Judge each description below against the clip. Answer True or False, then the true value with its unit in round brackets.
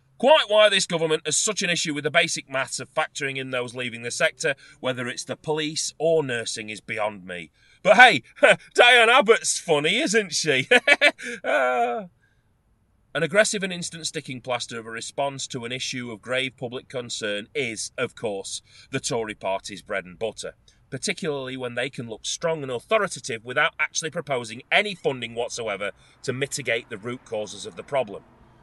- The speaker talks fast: False (170 wpm)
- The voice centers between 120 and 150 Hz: True (135 Hz)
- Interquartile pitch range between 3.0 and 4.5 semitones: False (5.6 semitones)